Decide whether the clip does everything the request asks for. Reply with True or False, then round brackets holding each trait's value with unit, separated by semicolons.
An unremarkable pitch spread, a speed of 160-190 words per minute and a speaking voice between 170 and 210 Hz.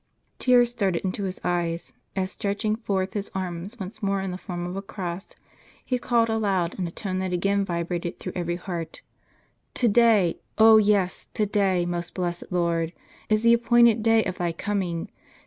True (3.4 semitones; 180 wpm; 190 Hz)